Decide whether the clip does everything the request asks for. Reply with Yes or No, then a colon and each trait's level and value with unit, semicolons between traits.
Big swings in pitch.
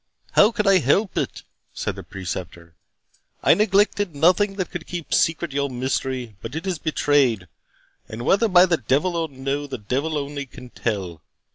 Yes: wide, 6.4 semitones